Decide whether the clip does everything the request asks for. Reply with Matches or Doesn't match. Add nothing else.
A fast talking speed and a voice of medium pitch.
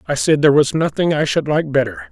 Matches